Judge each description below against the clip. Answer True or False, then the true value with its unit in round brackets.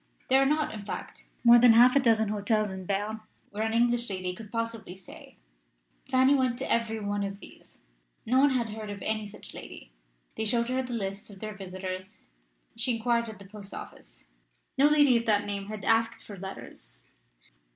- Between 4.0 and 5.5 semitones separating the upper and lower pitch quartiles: False (3.0 semitones)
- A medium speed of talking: True (195 wpm)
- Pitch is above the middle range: True (220 Hz)